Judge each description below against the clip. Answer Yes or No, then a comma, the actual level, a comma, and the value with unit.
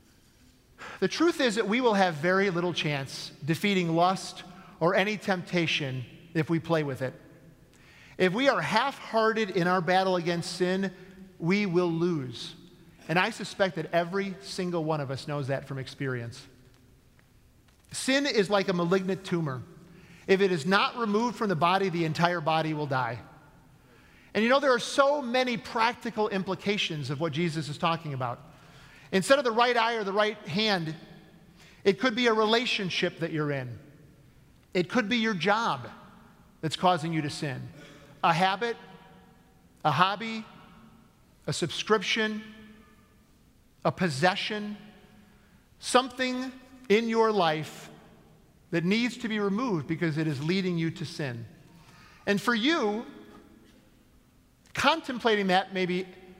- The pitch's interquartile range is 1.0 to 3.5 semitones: No, average, 4.9 semitones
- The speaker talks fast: No, average, 145 wpm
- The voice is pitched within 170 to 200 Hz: Yes, medium, 185 Hz